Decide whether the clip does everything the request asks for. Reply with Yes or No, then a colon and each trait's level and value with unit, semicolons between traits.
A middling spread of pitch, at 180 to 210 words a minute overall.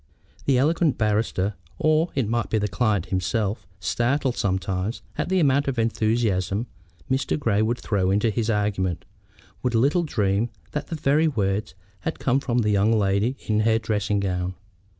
No: average, 4.6 semitones; average, 170 wpm